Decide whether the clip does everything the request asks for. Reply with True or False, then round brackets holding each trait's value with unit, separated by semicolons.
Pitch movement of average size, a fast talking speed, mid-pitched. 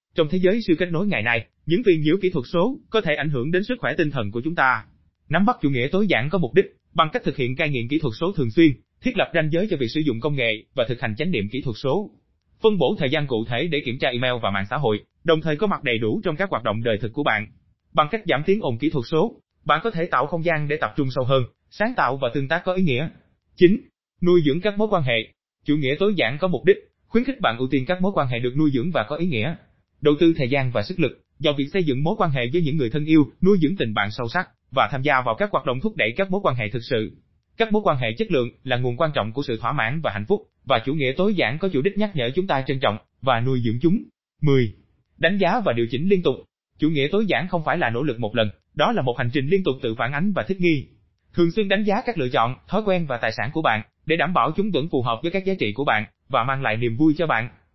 False (6.7 semitones; 300 wpm; 150 Hz)